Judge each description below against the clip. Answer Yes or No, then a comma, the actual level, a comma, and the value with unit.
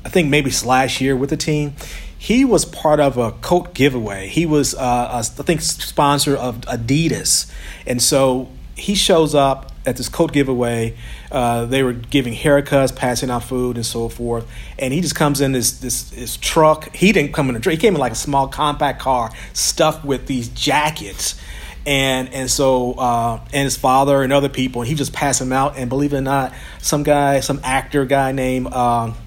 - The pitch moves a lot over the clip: No, average, 2.8 semitones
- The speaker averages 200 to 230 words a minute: Yes, fast, 205 wpm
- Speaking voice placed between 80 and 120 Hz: No, low, 135 Hz